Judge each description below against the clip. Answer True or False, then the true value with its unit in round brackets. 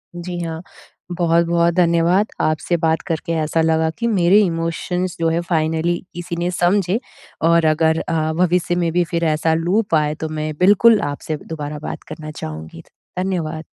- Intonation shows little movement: True (1.8 semitones)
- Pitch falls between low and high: True (170 Hz)